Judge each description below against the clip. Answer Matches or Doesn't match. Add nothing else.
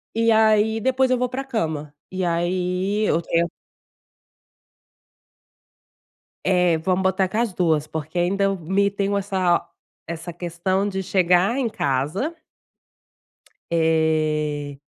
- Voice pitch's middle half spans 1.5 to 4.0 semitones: Matches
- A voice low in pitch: Doesn't match